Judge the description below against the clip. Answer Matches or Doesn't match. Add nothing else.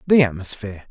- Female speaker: Doesn't match